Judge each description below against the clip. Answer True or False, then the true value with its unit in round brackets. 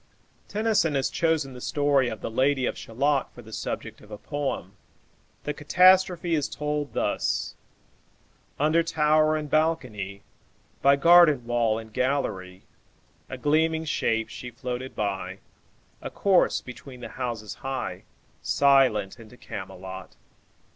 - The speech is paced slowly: True (130 wpm)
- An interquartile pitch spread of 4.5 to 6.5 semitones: True (5.4 semitones)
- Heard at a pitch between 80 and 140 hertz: True (135 Hz)